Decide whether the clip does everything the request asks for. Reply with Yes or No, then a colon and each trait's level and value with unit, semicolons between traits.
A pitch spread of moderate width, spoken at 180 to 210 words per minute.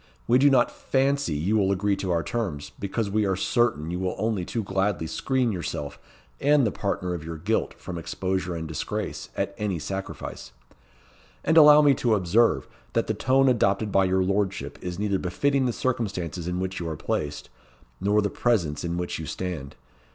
Yes: average, 4.9 semitones; average, 190 wpm